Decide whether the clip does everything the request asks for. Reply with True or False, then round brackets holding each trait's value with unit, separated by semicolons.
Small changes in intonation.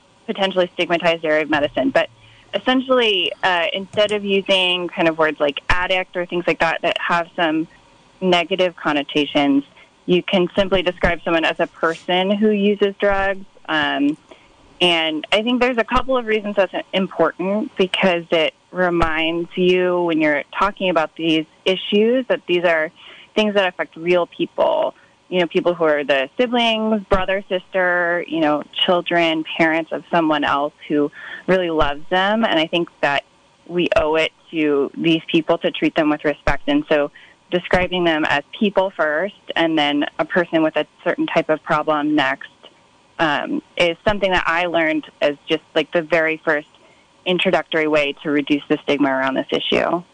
False (3.5 semitones)